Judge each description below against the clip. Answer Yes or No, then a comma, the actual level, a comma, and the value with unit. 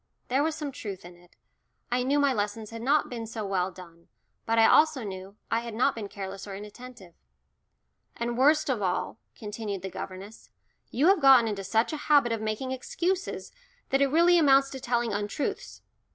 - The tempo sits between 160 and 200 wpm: Yes, average, 190 wpm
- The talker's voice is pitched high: Yes, high, 230 Hz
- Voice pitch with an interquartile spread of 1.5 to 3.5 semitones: No, average, 5.2 semitones